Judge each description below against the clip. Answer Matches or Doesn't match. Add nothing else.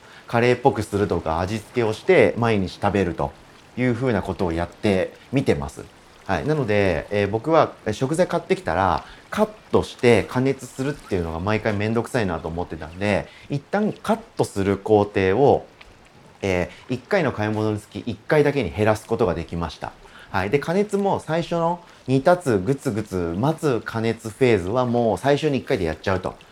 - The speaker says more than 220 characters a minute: Matches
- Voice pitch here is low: Matches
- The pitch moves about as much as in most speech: Doesn't match